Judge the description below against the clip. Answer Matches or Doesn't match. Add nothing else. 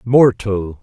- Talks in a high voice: Doesn't match